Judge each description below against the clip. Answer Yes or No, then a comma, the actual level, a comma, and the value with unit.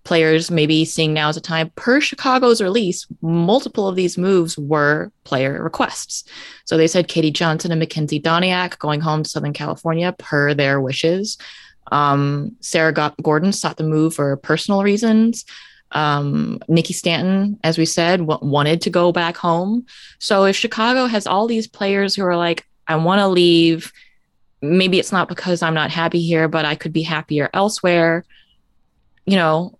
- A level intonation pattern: No, average, 3.5 semitones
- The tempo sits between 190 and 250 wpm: No, average, 170 wpm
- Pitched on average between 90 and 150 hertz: No, medium, 165 Hz